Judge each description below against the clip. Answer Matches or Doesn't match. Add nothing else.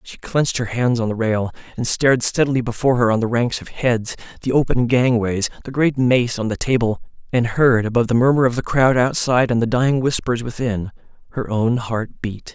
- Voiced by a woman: Doesn't match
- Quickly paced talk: Matches